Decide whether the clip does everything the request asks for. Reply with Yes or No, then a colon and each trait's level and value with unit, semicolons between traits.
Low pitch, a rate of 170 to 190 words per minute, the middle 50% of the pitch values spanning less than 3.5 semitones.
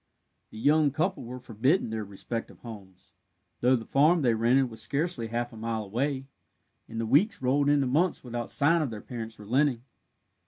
No: low, 125 Hz; average, 180 wpm; average, 4.1 semitones